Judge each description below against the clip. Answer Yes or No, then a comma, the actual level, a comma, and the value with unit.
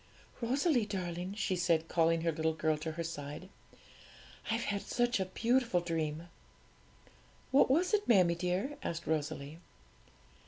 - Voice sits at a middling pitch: Yes, medium, 175 Hz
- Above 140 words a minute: No, slow, 135 wpm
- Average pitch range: No, wide, 5.8 semitones